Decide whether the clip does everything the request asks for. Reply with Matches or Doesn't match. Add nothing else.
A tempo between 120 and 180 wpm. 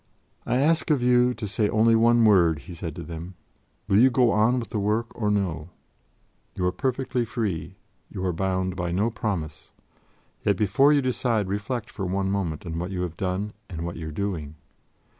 Doesn't match